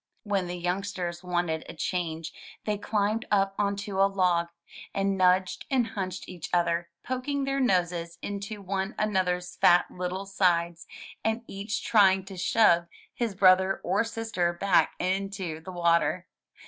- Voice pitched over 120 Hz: Yes, high, 190 Hz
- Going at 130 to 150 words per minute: Yes, average, 145 wpm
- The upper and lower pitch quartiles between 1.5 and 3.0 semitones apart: Yes, narrow, 2.5 semitones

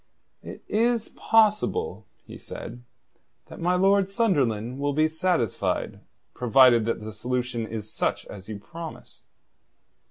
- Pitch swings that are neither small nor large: No, wide, 9.0 semitones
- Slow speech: Yes, slow, 125 wpm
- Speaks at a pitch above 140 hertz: No, low, 135 Hz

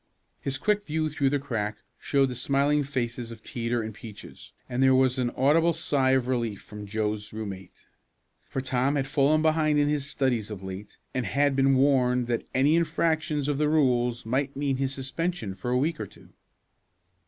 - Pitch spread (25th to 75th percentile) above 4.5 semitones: No, average, 3.6 semitones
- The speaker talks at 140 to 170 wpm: No, average, 190 wpm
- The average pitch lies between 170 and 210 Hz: No, low, 130 Hz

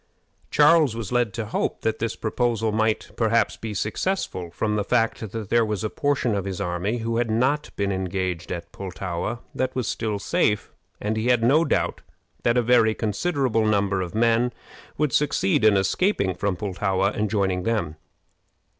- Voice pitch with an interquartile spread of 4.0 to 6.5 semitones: No, average, 3.3 semitones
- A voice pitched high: No, low, 110 Hz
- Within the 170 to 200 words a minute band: Yes, average, 175 wpm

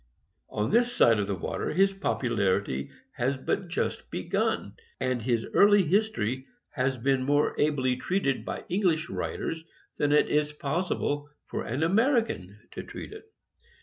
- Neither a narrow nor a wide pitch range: No, wide, 7.1 semitones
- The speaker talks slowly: No, average, 150 wpm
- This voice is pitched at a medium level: Yes, medium, 145 Hz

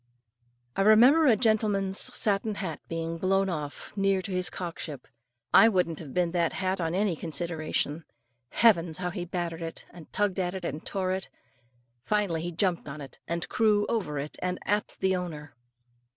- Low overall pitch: No, medium, 180 Hz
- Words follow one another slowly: No, average, 175 wpm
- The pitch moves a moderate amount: Yes, average, 3.1 semitones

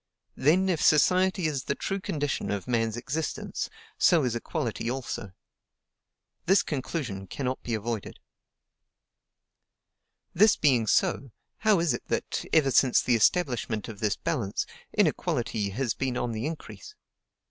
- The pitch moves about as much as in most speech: No, wide, 6.0 semitones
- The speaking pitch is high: No, low, 130 Hz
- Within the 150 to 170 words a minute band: No, slow, 135 wpm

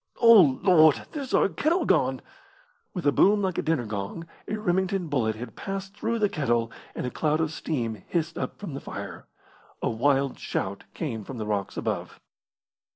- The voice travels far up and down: Yes, wide, 8.5 semitones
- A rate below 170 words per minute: No, average, 180 wpm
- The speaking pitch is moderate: Yes, medium, 155 Hz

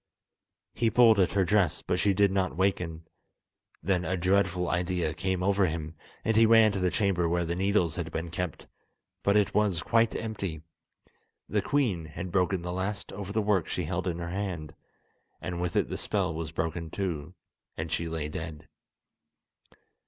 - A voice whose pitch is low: Yes, very low, 90 Hz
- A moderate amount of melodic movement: Yes, average, 3.0 semitones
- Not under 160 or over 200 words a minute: Yes, average, 180 wpm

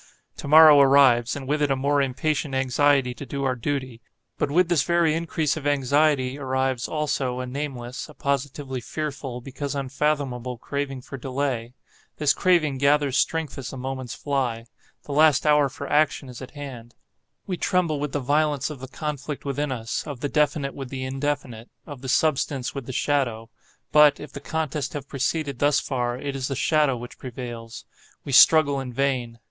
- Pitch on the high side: No, medium, 140 Hz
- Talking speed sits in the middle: Yes, average, 175 wpm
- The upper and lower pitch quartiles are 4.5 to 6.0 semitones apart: No, narrow, 2.4 semitones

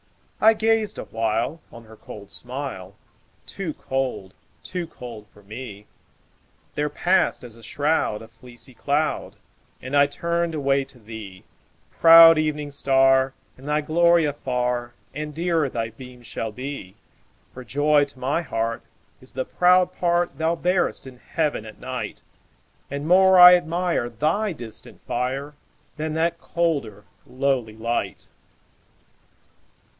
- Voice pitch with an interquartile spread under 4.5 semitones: No, wide, 5.4 semitones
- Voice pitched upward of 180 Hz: No, medium, 140 Hz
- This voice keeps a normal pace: No, slow, 130 wpm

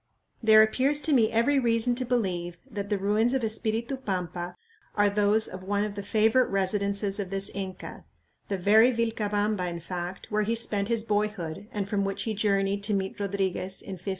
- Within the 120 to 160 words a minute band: No, average, 190 wpm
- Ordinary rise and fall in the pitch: No, narrow, 2.3 semitones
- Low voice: No, high, 205 Hz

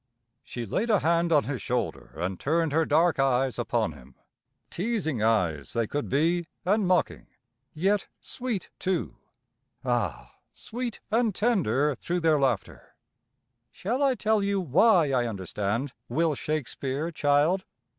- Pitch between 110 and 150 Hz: No, medium, 160 Hz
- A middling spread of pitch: No, wide, 6.7 semitones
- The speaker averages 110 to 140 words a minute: Yes, slow, 135 wpm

